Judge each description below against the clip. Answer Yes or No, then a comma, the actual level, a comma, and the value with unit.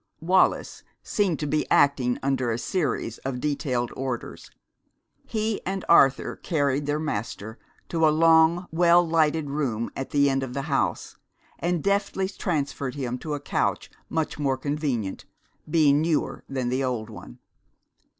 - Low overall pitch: No, medium, 145 Hz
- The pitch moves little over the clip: No, average, 3.7 semitones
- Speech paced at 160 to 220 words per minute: No, average, 150 wpm